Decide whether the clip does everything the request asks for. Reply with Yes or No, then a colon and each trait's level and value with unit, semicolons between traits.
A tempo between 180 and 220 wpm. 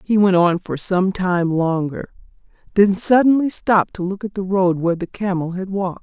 Yes: average, 200 wpm